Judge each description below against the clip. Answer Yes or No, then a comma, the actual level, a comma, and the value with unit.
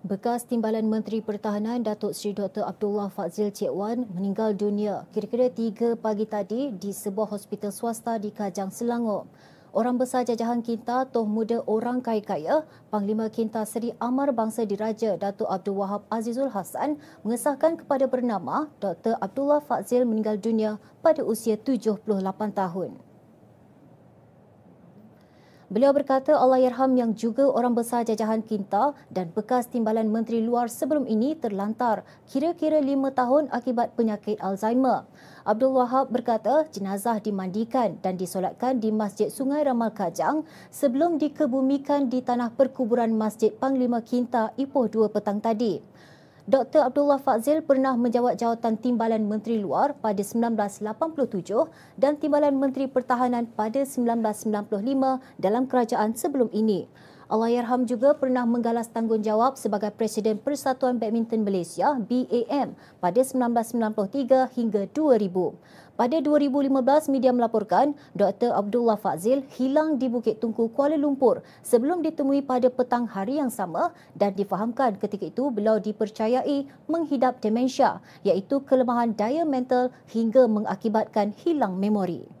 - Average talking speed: Yes, average, 130 wpm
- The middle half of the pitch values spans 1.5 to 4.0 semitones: Yes, average, 3.6 semitones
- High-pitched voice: Yes, high, 235 Hz